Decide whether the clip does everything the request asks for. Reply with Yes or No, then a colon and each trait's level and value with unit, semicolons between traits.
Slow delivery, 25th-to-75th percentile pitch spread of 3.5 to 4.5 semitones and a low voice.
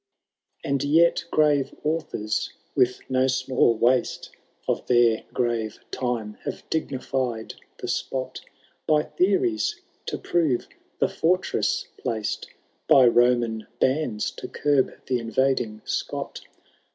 Yes: slow, 110 wpm; average, 3.9 semitones; low, 130 Hz